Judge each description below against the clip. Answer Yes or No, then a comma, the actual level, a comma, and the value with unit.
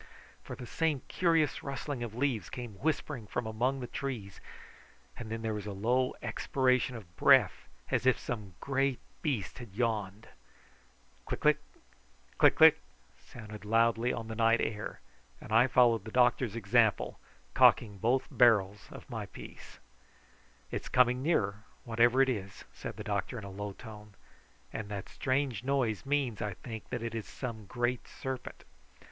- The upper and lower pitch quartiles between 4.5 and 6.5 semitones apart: No, average, 3.2 semitones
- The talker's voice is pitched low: Yes, low, 115 Hz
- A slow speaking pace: No, average, 160 wpm